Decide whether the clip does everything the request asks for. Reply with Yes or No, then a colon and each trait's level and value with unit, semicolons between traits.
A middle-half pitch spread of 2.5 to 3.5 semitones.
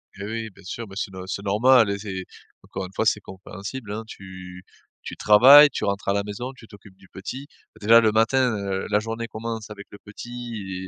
Yes: average, 2.8 semitones